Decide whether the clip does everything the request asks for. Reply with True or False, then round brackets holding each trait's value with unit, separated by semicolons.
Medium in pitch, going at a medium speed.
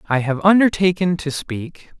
True (165 Hz; 150 wpm)